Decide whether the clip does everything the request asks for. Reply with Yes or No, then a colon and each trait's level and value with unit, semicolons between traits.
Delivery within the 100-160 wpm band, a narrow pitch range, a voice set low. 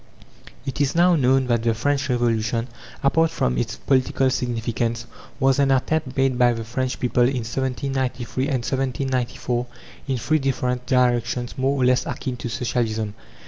Yes: average, 155 wpm; narrow, 2.1 semitones; low, 125 Hz